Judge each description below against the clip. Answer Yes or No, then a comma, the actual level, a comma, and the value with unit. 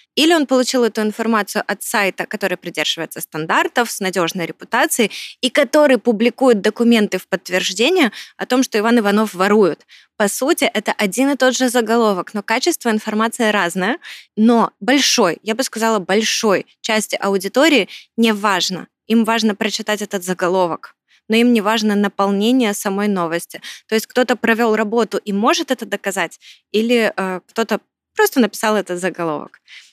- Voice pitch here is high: Yes, high, 220 Hz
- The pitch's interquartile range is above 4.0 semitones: No, average, 3.4 semitones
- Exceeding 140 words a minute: Yes, average, 150 wpm